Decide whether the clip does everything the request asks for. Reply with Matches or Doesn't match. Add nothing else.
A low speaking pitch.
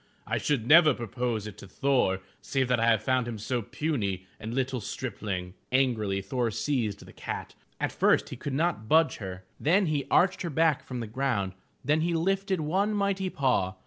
Matches